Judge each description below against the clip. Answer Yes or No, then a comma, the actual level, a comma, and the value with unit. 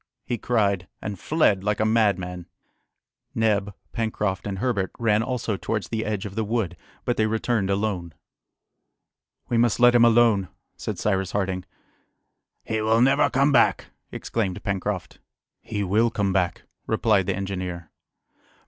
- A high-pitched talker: No, low, 105 Hz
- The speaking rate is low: No, average, 145 wpm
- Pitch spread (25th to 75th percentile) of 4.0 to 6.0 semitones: No, average, 2.9 semitones